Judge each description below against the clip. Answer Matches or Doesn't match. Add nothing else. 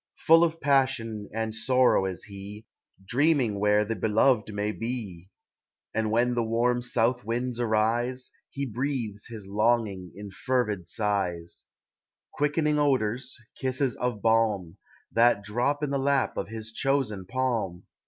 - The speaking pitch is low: Matches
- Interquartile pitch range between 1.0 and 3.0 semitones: Doesn't match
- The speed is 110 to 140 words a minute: Matches